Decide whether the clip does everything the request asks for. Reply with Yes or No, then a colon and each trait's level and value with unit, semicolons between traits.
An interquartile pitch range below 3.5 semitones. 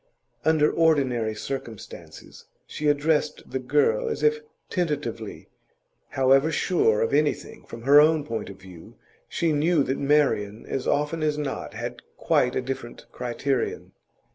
No: average, 4.2 semitones